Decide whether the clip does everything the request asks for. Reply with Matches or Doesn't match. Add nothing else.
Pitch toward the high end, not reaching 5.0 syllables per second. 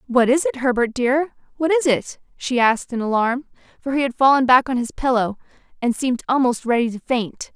Doesn't match